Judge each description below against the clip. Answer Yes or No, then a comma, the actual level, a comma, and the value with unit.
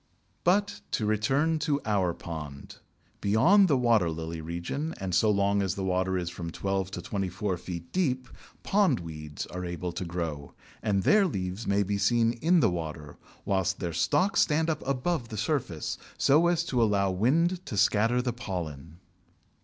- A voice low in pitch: Yes, low, 100 Hz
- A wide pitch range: Yes, wide, 7.4 semitones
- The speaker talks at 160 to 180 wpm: Yes, average, 170 wpm